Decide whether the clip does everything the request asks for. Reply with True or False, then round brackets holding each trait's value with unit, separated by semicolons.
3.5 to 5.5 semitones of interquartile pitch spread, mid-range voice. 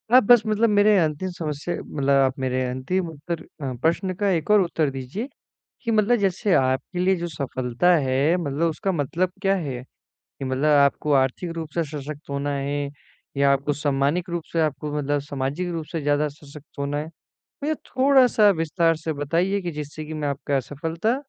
True (4.4 semitones; 155 Hz)